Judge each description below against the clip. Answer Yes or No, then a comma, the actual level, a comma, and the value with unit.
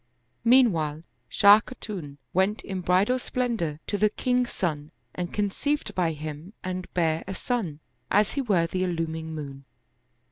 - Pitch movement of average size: Yes, average, 4.9 semitones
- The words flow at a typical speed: Yes, average, 145 wpm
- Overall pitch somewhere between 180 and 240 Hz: Yes, medium, 185 Hz